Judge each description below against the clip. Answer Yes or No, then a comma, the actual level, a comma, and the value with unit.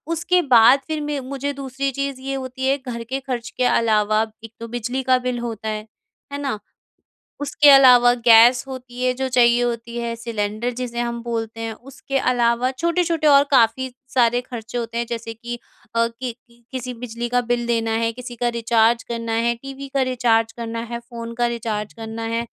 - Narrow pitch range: Yes, narrow, 2.1 semitones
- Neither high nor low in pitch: No, high, 240 Hz